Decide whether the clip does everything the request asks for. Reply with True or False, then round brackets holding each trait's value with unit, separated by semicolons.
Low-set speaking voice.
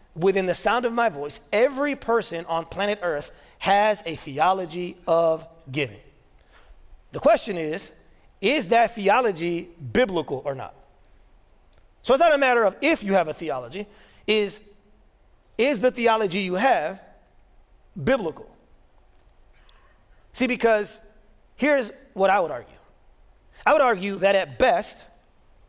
False (200 Hz)